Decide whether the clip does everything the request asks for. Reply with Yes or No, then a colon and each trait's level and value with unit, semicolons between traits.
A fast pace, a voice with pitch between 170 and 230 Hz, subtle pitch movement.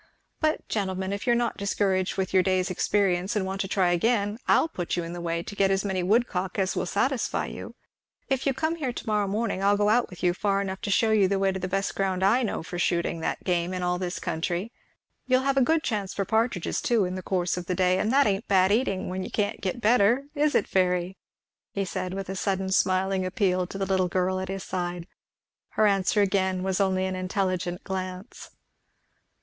Yes: fast, 230 wpm; high, 190 Hz; narrow, 2.1 semitones